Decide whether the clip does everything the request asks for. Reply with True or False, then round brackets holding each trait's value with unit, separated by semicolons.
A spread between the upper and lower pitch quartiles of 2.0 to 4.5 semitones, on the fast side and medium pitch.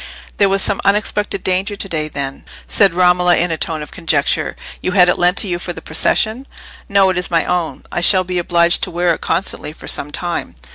True (2.5 semitones; 225 wpm; 180 Hz)